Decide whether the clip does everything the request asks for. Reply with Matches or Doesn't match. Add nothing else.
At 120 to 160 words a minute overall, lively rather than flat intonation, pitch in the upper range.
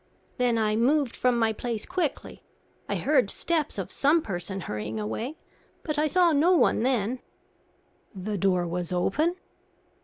Matches